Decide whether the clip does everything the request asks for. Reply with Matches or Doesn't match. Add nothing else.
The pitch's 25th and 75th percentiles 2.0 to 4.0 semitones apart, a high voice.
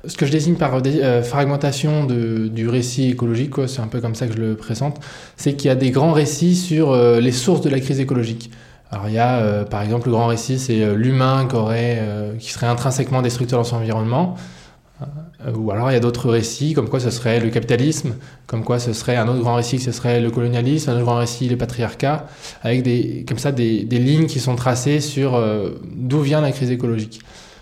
Doesn't match